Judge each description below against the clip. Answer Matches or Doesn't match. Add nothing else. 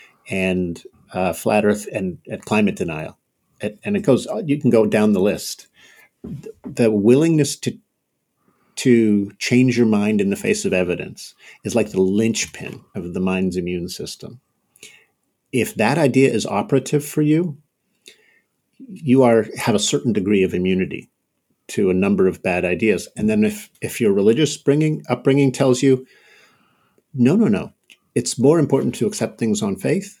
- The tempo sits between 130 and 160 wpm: Matches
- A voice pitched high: Doesn't match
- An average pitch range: Doesn't match